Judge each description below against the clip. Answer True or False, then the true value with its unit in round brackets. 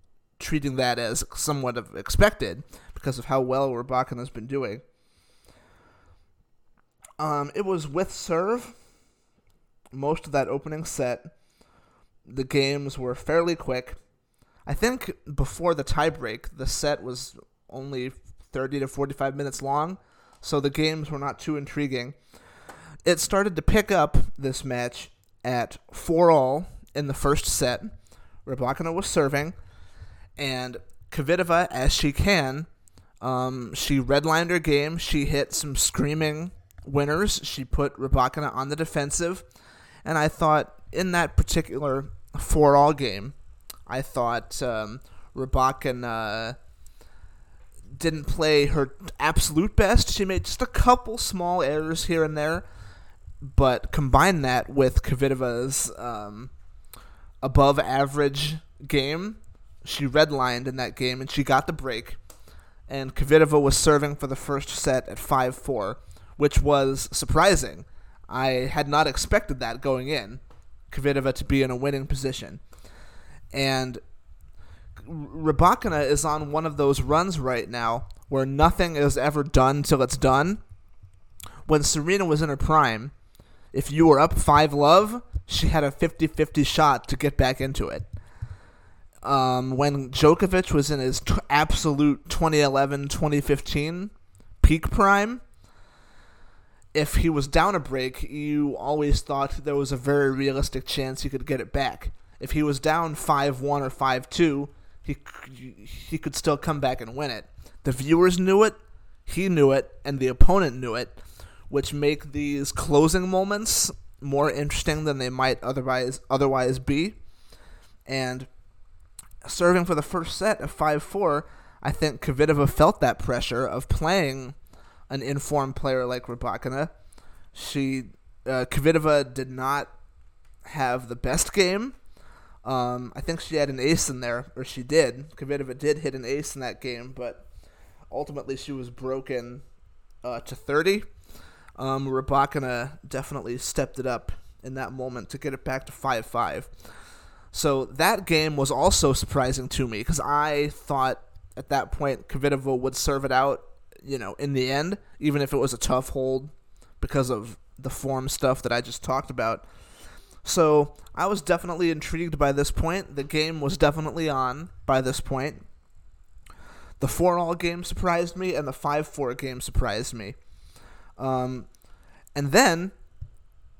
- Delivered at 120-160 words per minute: True (145 wpm)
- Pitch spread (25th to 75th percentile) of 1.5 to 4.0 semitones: True (3.2 semitones)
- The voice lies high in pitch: False (140 Hz)